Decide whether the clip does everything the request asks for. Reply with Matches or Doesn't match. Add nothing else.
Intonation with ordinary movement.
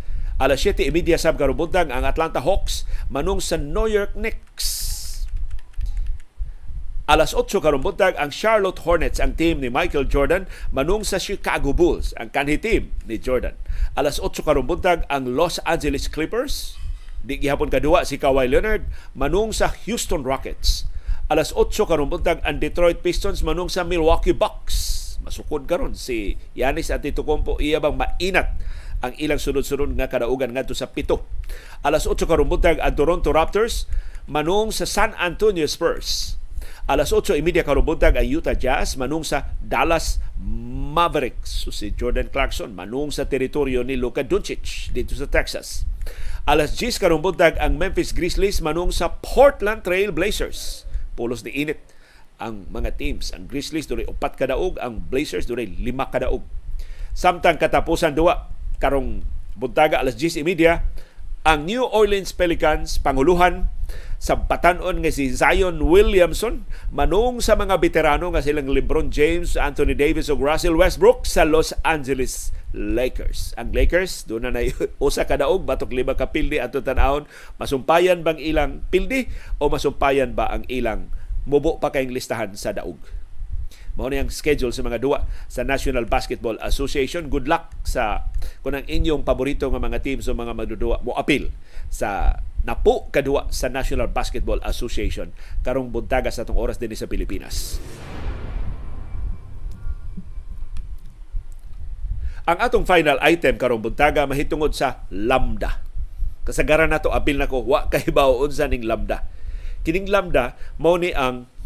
Doesn't match